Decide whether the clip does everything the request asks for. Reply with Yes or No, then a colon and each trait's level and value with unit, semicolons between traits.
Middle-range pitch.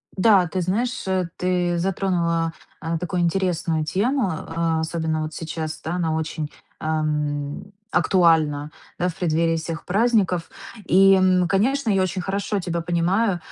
Yes: medium, 170 Hz